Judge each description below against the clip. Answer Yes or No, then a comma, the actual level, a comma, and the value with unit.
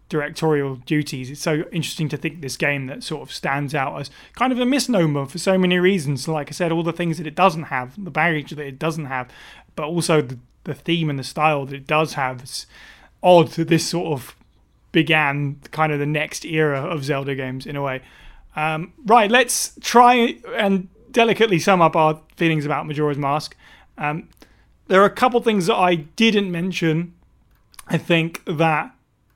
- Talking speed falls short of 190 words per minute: No, average, 195 wpm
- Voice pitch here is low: No, medium, 155 Hz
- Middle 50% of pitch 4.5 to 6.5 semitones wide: No, average, 3.6 semitones